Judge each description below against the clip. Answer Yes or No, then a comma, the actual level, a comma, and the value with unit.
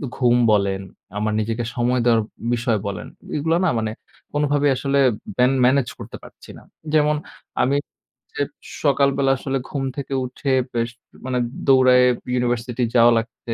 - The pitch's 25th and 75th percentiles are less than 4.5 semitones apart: Yes, average, 2.9 semitones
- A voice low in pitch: Yes, low, 125 Hz